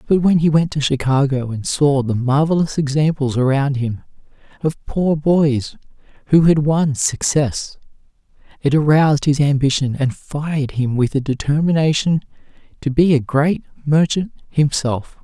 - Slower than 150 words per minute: Yes, average, 140 wpm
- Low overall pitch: No, medium, 145 Hz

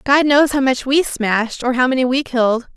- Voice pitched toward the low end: No, very high, 260 Hz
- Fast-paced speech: Yes, fast, 240 wpm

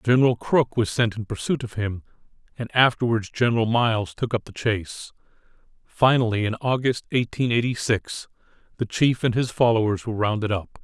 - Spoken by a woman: No, male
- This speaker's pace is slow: No, average, 165 wpm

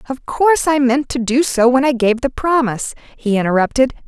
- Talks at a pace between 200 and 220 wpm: Yes, fast, 205 wpm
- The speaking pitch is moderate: No, very high, 255 Hz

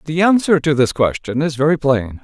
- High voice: No, medium, 145 Hz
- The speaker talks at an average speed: No, fast, 215 wpm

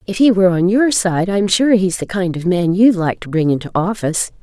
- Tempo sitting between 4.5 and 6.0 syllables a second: Yes, 5.5 syllables/s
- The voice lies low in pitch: No, high, 190 Hz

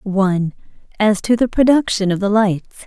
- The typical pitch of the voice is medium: No, high, 205 Hz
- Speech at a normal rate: Yes, average, 170 wpm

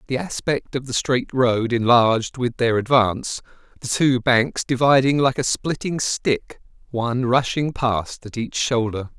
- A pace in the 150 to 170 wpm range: Yes, average, 155 wpm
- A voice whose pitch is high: No, low, 125 Hz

